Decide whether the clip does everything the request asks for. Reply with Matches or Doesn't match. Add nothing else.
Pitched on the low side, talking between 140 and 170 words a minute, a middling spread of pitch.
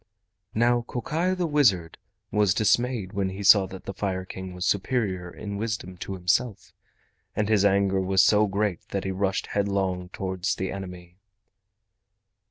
Doesn't match